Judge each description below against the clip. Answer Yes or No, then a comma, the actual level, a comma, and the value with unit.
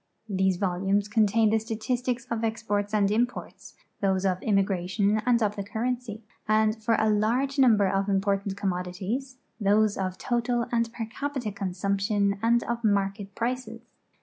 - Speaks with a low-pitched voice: No, high, 210 Hz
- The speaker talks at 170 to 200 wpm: No, average, 150 wpm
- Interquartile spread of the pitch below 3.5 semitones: Yes, average, 2.8 semitones